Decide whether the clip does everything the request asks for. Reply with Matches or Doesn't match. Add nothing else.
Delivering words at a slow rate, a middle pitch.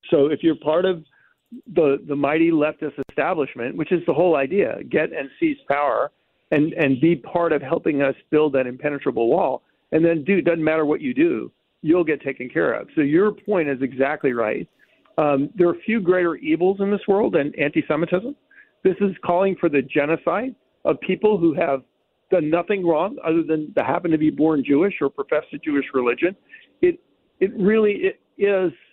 Doesn't match